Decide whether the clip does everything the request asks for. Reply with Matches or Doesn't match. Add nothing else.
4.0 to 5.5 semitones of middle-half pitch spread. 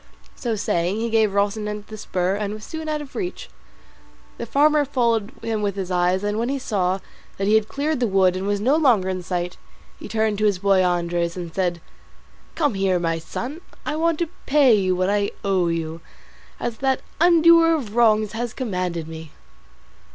Matches